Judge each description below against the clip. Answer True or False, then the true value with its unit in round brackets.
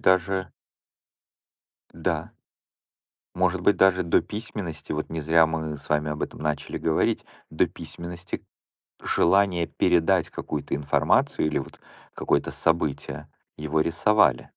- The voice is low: True (85 Hz)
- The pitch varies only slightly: False (3.3 semitones)